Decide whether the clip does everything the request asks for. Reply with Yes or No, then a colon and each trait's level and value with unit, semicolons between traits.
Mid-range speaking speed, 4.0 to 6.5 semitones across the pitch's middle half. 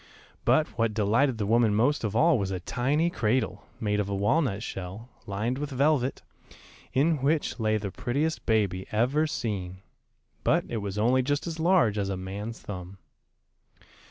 Yes: average, 165 wpm; wide, 5.6 semitones